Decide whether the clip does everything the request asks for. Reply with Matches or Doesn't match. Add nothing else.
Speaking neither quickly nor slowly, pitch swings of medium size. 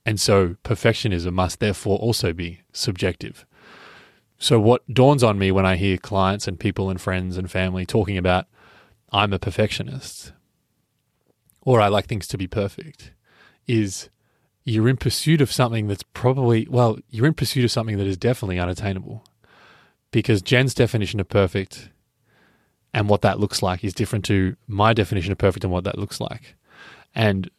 Matches